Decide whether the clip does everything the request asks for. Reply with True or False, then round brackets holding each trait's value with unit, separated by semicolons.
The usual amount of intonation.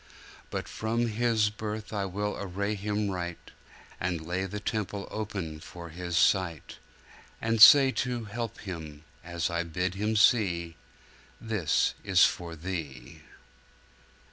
True (3.8 semitones)